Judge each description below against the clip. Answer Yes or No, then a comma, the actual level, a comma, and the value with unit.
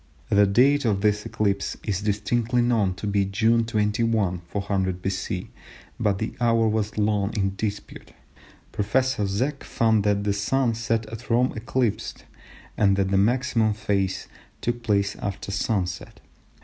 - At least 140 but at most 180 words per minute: Yes, average, 150 wpm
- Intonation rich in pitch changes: No, narrow, 2.6 semitones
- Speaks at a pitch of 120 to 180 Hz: No, low, 105 Hz